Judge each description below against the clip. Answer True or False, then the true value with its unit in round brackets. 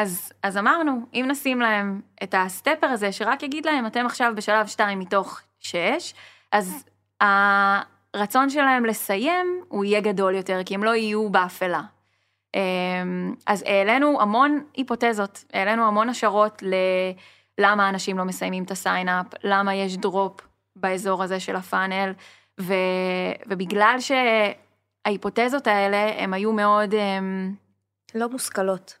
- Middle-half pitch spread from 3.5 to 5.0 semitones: False (3.1 semitones)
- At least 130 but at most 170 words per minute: False (120 wpm)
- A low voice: False (200 Hz)